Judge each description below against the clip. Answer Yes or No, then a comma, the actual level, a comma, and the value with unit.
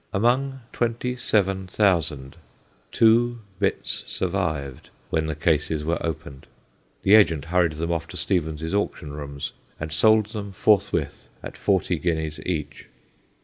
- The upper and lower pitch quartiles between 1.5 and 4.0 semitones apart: No, average, 5.0 semitones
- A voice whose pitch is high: No, very low, 85 Hz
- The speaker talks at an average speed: No, slow, 130 wpm